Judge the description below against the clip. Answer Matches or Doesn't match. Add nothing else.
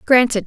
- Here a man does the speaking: Doesn't match